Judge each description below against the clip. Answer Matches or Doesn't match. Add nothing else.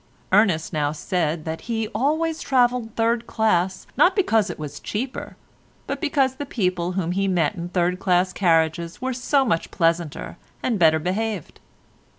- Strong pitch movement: Matches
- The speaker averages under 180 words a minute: Matches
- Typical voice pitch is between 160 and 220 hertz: Matches